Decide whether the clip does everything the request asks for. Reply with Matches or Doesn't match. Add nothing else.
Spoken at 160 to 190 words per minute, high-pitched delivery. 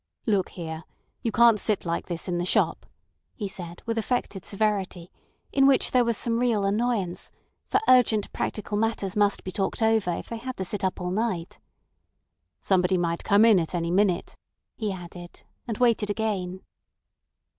Matches